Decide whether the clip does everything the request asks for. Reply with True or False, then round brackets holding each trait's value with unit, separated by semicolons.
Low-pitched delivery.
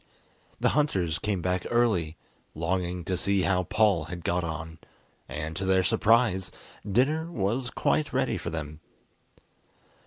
True (95 Hz)